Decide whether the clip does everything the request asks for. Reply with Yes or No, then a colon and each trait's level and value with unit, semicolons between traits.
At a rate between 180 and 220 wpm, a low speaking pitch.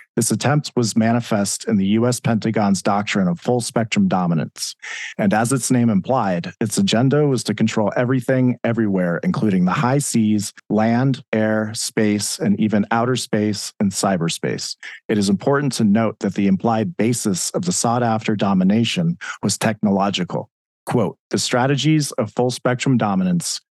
No: average, 155 wpm; low, 115 Hz